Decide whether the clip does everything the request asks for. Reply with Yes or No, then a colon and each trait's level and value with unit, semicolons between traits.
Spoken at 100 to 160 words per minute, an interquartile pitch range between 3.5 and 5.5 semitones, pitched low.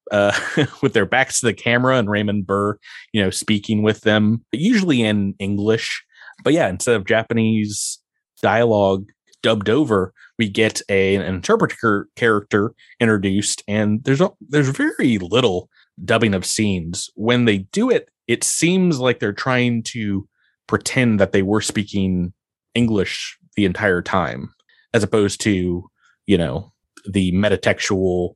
No: average, 145 wpm; average, 2.7 semitones; low, 105 Hz